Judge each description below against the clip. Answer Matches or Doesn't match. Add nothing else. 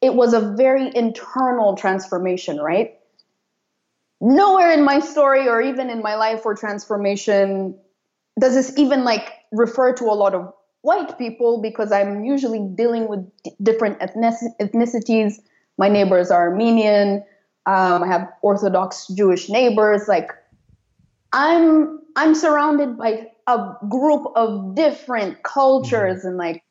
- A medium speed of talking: Doesn't match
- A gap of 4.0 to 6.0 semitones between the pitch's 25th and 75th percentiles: Matches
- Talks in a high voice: Matches